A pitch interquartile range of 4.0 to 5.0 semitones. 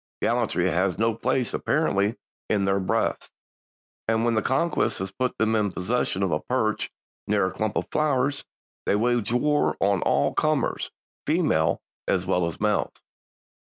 Yes: average, 4.3 semitones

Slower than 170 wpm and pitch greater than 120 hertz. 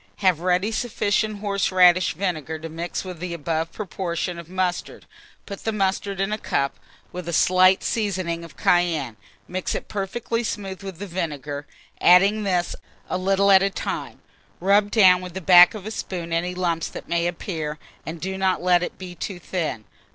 No: average, 180 wpm; medium, 185 Hz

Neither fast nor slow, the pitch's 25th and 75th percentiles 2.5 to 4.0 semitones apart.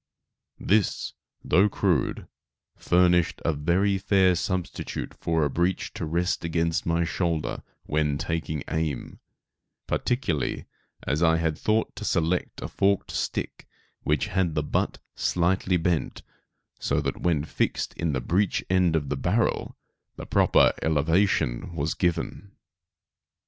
No: slow, 130 wpm; average, 2.9 semitones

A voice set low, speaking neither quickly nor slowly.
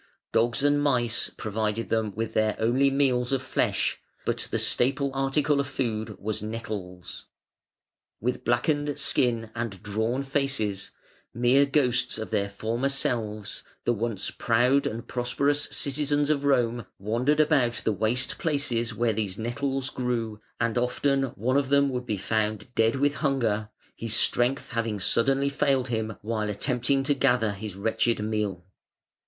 Yes: low, 120 Hz; average, 150 wpm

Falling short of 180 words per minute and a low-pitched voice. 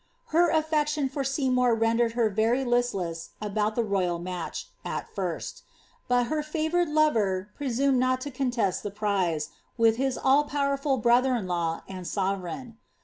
No: average, 155 wpm; high, 240 Hz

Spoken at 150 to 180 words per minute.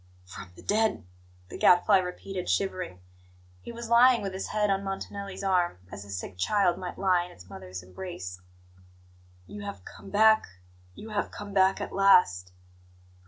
Yes: average, 165 wpm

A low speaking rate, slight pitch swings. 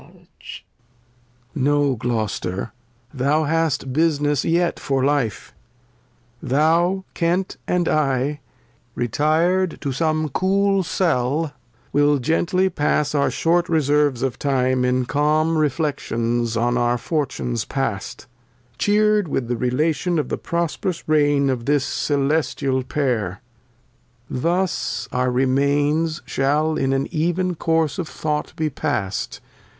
No: slow, 115 wpm; average, 4.0 semitones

